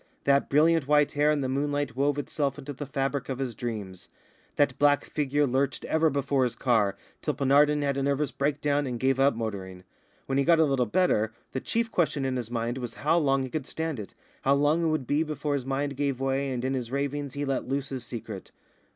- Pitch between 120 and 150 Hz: Yes, medium, 140 Hz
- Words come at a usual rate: No, fast, 225 wpm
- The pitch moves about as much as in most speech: No, narrow, 2.2 semitones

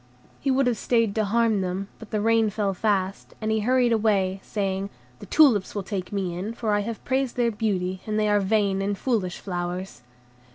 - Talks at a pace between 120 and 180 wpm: No, fast, 205 wpm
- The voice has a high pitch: Yes, high, 210 Hz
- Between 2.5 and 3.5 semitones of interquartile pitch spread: Yes, average, 2.8 semitones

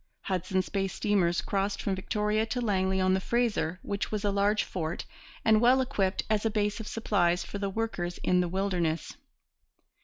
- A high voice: Yes, high, 200 Hz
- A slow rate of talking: No, average, 180 wpm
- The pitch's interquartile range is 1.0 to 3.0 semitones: Yes, narrow, 2.4 semitones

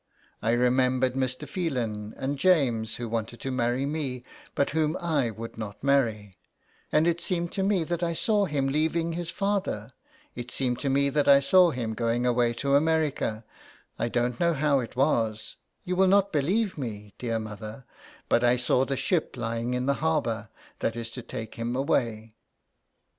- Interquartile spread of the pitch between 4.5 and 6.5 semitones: Yes, average, 5.3 semitones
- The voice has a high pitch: No, low, 130 Hz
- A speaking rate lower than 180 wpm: No, average, 190 wpm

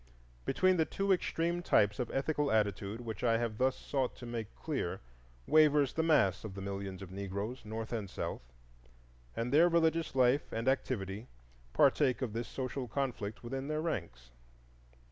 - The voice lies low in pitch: Yes, low, 120 Hz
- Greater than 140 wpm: Yes, average, 165 wpm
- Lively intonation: Yes, wide, 5.8 semitones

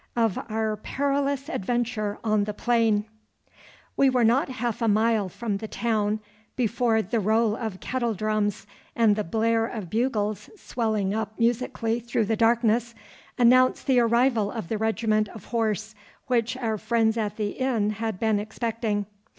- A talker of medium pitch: No, high, 225 Hz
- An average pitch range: No, narrow, 1.9 semitones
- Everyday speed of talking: Yes, average, 150 wpm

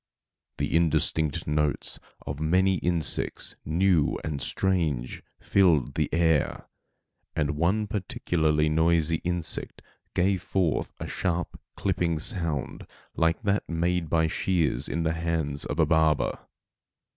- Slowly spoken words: Yes, slow, 120 wpm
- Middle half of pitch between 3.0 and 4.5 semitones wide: No, narrow, 2.4 semitones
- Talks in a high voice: No, very low, 80 Hz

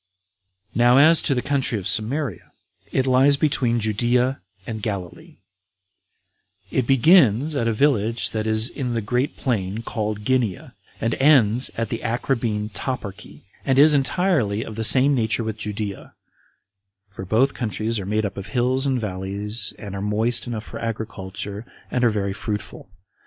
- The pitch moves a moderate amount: Yes, average, 3.7 semitones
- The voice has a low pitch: Yes, low, 115 Hz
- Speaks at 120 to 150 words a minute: No, average, 160 wpm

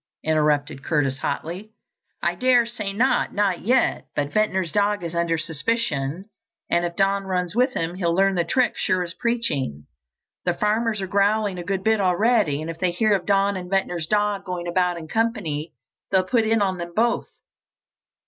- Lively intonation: No, average, 3.8 semitones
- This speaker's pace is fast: No, average, 175 wpm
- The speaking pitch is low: No, high, 190 Hz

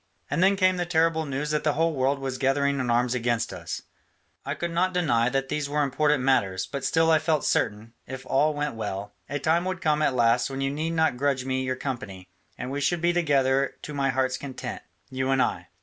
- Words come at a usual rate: No, fast, 230 wpm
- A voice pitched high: No, medium, 140 Hz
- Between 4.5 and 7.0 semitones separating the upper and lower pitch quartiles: No, average, 3.3 semitones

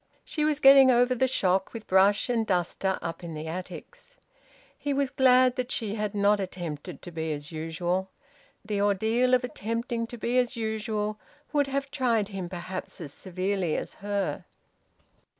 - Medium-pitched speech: No, high, 210 Hz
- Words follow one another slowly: No, average, 170 wpm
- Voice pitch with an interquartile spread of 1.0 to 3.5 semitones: No, average, 5.1 semitones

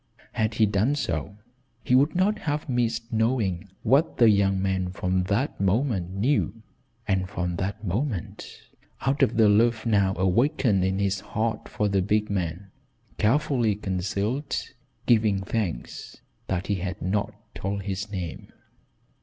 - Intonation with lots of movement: No, average, 3.6 semitones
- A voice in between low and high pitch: No, low, 105 Hz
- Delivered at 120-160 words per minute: Yes, average, 145 wpm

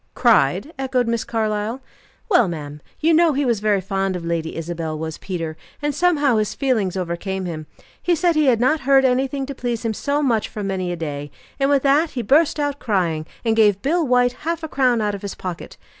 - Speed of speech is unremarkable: No, fast, 215 wpm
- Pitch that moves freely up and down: Yes, wide, 7.1 semitones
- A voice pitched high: Yes, high, 230 Hz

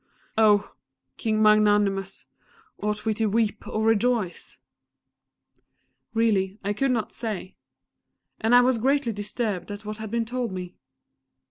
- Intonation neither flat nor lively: No, narrow, 2.0 semitones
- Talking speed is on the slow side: Yes, slow, 130 wpm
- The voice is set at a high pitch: Yes, high, 215 Hz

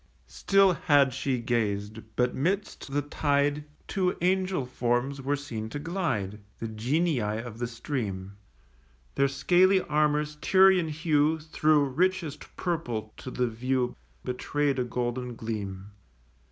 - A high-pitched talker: No, medium, 140 Hz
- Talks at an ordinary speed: No, slow, 125 wpm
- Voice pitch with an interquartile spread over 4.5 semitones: Yes, average, 4.9 semitones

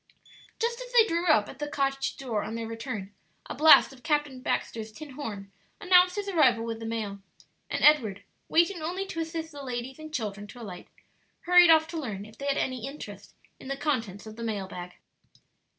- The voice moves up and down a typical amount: No, wide, 6.2 semitones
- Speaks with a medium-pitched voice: No, very high, 270 Hz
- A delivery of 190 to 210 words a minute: Yes, average, 200 wpm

